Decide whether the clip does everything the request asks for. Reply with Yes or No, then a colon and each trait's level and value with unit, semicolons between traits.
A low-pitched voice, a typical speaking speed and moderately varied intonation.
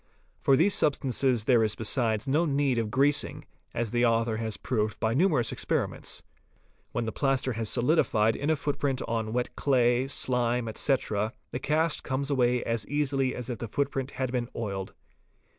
Yes: low, 125 Hz; average, 175 wpm; average, 3.3 semitones